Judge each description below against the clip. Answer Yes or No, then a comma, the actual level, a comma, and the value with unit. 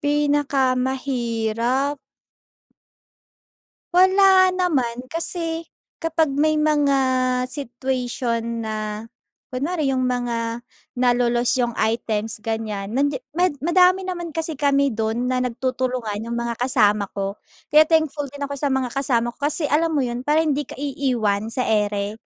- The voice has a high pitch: Yes, very high, 255 Hz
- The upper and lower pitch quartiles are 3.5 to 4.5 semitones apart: Yes, average, 4.2 semitones